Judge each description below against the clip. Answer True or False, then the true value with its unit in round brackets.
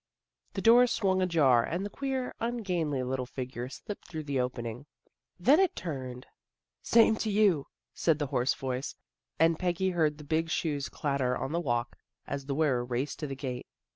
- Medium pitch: True (150 Hz)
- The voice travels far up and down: True (5.9 semitones)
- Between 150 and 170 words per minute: False (180 wpm)